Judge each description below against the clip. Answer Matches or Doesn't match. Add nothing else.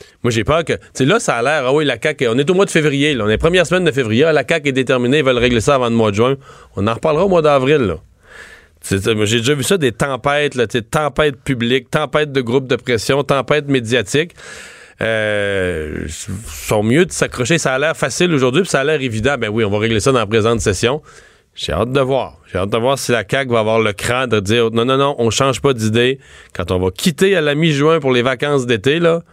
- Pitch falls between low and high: Doesn't match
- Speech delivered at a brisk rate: Matches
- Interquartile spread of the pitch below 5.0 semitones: Matches